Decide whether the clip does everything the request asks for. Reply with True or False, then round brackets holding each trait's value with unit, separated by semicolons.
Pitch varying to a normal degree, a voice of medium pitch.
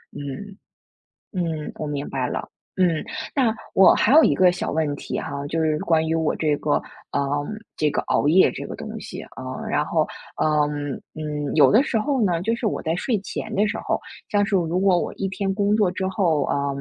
True (5.0 semitones; 170 Hz)